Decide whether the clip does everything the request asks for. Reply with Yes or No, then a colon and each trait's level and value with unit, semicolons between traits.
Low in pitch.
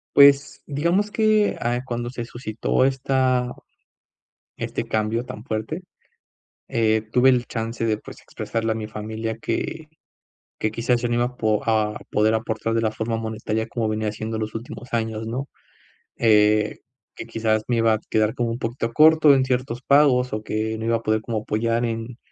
Yes: low, 115 Hz